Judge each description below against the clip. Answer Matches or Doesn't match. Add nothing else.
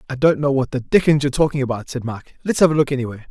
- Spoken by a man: Matches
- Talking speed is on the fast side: Matches